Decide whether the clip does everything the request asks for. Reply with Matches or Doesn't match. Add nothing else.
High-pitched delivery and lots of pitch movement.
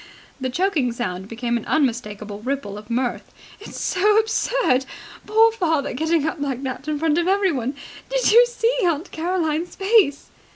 Matches